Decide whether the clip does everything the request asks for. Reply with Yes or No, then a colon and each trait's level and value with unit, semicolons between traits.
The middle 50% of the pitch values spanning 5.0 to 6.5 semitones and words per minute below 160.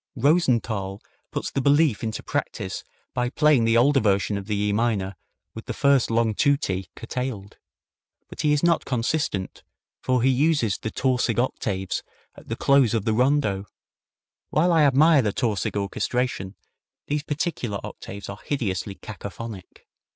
Yes: wide, 5.5 semitones; average, 150 wpm